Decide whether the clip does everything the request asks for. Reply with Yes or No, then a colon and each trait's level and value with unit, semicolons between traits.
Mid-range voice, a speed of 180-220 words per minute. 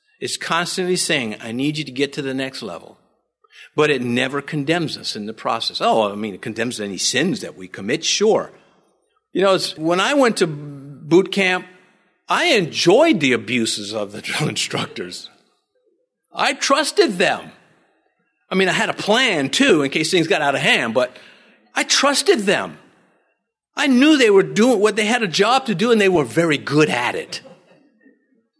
Yes: medium, 180 Hz; average, 185 wpm